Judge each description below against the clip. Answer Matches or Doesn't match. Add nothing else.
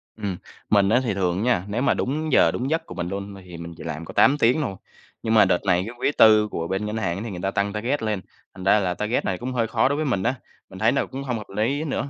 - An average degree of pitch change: Matches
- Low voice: Matches